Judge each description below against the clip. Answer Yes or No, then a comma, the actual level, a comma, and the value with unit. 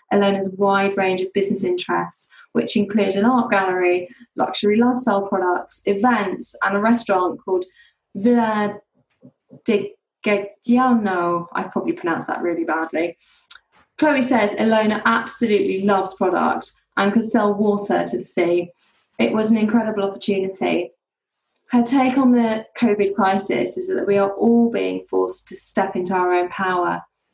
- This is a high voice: Yes, high, 200 Hz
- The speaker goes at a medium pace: Yes, average, 145 wpm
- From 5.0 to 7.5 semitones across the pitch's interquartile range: No, average, 3.6 semitones